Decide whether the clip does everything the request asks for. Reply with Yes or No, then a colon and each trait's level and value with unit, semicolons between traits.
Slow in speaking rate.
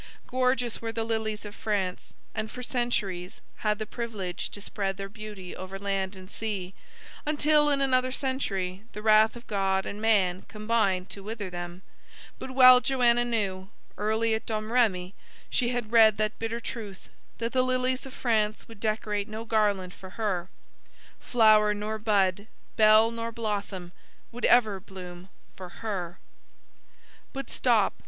No: average, 150 wpm